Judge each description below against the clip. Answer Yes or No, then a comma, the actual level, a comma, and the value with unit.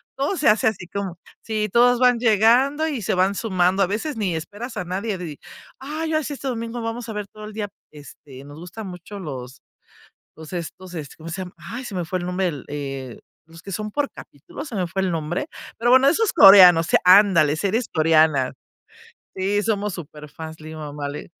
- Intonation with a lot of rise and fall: Yes, wide, 5.8 semitones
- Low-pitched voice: No, high, 190 Hz